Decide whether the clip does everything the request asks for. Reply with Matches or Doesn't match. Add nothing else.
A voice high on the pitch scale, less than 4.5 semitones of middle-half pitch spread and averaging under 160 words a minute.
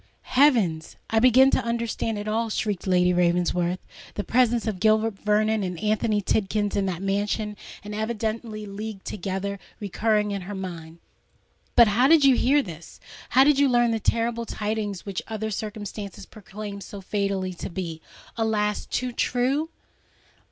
Matches